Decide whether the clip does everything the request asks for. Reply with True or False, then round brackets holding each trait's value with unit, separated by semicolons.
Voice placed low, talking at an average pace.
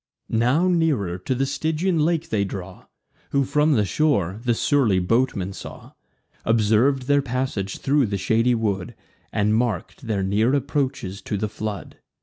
True (115 Hz; 150 wpm)